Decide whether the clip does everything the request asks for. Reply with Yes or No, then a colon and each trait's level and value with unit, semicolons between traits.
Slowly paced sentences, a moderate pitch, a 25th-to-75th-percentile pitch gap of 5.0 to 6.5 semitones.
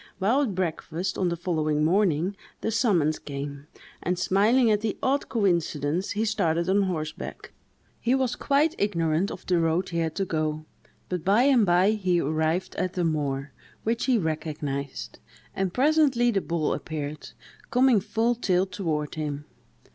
No: average, 160 wpm; medium, 180 Hz; wide, 5.5 semitones